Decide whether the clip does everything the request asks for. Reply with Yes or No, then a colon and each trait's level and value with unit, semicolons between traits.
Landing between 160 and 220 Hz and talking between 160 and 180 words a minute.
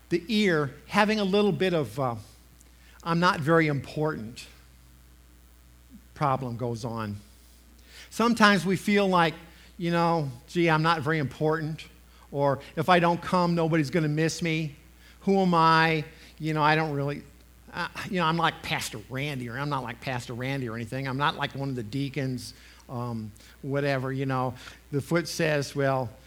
No: medium, 140 Hz; average, 170 wpm